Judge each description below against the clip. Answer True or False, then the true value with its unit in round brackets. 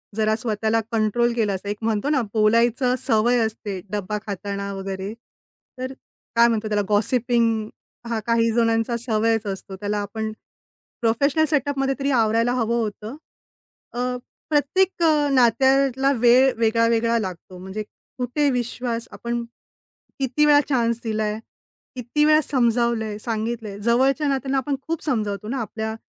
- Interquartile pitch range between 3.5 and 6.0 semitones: False (2.9 semitones)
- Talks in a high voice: True (230 Hz)